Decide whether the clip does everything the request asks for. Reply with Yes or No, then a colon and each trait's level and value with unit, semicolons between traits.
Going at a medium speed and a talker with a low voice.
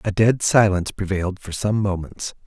Yes: average, 170 wpm; low, 100 Hz